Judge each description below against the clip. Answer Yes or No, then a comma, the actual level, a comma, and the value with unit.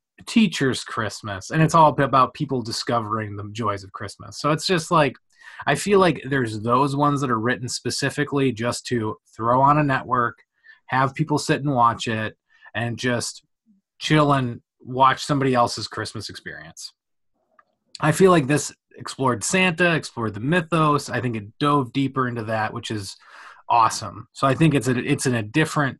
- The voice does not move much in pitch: No, average, 4.2 semitones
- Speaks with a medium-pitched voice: No, low, 130 Hz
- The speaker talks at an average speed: Yes, average, 175 wpm